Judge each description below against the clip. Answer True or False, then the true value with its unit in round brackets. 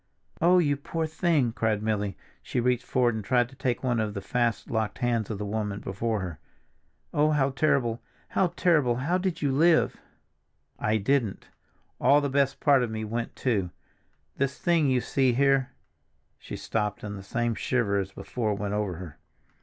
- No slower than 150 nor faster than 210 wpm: True (180 wpm)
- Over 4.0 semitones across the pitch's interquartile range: True (4.5 semitones)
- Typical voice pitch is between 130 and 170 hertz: False (120 Hz)